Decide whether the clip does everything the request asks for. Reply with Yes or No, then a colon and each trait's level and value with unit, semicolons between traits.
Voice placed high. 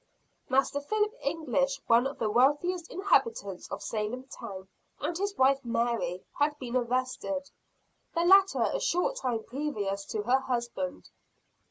Yes: very high, 265 Hz